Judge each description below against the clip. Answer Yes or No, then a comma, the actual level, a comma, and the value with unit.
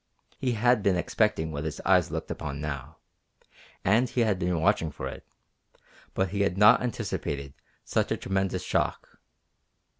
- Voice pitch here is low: Yes, very low, 95 Hz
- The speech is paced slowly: No, average, 155 wpm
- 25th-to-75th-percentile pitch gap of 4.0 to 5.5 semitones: Yes, average, 5.2 semitones